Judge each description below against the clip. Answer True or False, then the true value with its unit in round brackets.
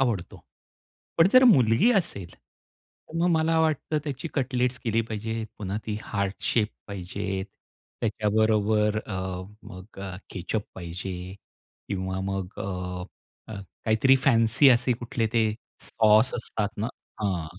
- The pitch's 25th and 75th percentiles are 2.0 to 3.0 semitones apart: False (4.0 semitones)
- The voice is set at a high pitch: False (110 Hz)